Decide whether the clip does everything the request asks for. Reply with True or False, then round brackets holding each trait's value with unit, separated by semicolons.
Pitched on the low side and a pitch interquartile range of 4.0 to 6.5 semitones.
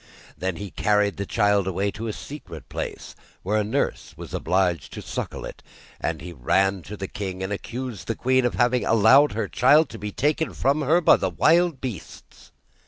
True (105 Hz; 5.2 semitones)